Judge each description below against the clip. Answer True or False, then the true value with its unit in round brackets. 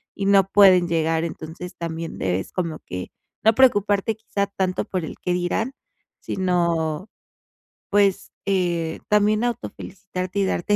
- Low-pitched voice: False (185 Hz)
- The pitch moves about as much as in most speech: True (3.3 semitones)